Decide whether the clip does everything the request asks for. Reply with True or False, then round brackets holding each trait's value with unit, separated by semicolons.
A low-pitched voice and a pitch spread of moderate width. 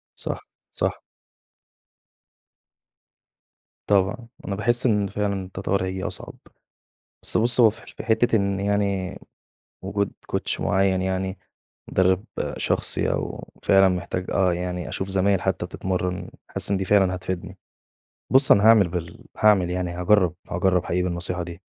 False (95 Hz; 1.9 semitones)